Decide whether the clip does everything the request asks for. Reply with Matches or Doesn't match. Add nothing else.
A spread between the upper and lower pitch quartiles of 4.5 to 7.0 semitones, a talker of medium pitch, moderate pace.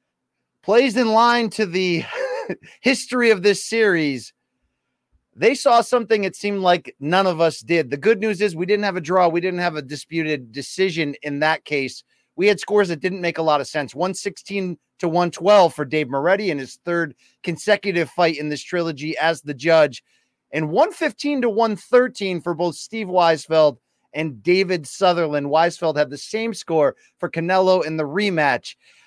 Matches